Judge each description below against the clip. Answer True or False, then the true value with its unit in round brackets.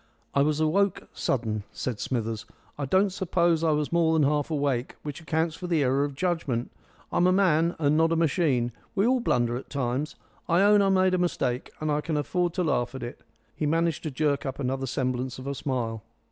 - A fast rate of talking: True (215 wpm)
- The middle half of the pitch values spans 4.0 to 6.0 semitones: True (4.5 semitones)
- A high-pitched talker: False (150 Hz)